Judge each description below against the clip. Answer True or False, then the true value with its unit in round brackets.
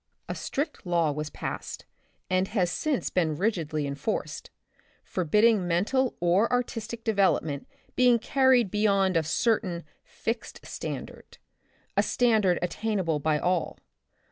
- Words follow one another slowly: True (115 wpm)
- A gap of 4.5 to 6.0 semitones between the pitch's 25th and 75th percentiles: True (5.2 semitones)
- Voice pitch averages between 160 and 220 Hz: True (190 Hz)